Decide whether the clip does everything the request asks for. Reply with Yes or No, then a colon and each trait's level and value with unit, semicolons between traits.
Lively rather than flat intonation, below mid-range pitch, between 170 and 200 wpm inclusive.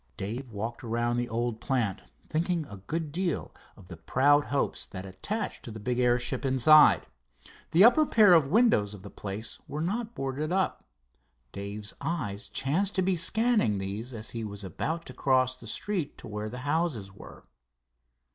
Yes: wide, 7.7 semitones; low, 130 Hz; average, 175 wpm